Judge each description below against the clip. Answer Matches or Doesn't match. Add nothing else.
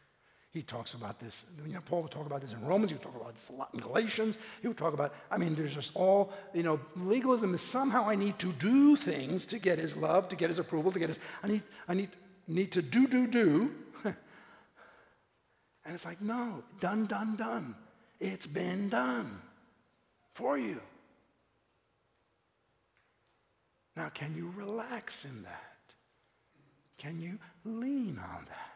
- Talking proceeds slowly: Doesn't match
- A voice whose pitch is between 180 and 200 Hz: Matches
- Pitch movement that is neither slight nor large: Doesn't match